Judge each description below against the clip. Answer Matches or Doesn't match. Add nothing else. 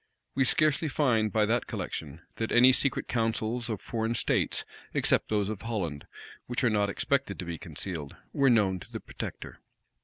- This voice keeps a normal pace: Matches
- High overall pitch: Doesn't match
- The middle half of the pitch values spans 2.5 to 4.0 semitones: Matches